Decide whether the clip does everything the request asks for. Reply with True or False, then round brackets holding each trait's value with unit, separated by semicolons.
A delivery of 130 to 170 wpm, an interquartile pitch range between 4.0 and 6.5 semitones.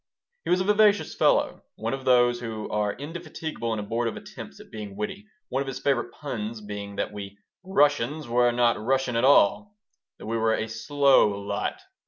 False (185 wpm; 5.0 semitones)